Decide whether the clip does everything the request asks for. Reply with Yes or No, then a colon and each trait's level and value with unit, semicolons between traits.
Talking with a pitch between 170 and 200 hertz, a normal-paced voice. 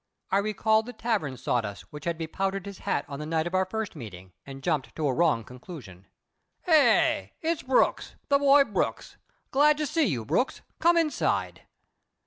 Yes: high, 190 Hz; average, 175 wpm